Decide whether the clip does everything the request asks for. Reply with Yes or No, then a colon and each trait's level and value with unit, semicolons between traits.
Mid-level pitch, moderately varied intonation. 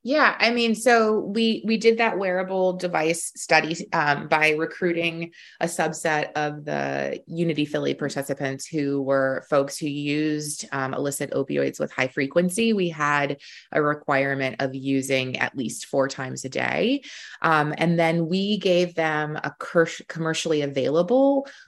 Yes: medium, 155 Hz; average, 4.6 semitones